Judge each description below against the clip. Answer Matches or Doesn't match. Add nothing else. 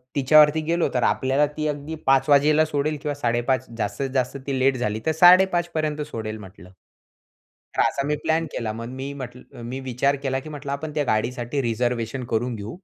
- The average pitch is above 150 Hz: Doesn't match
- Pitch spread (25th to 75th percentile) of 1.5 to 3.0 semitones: Doesn't match